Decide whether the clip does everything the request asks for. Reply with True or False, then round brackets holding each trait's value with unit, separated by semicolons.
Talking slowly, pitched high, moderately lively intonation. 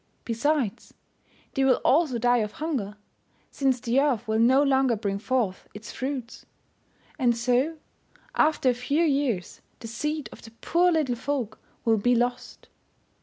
False (150 wpm; 250 Hz; 3.7 semitones)